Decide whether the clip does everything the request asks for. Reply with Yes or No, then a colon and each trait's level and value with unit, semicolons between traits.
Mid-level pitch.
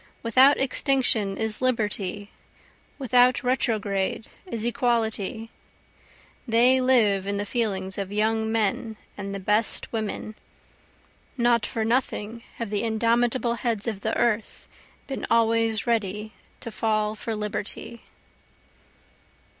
No: high, 225 Hz